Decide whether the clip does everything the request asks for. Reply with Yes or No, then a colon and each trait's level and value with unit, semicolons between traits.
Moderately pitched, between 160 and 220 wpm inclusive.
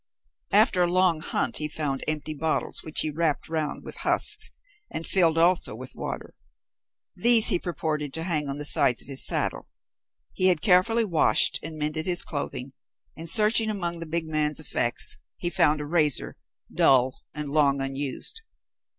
Yes: medium, 155 Hz; average, 170 wpm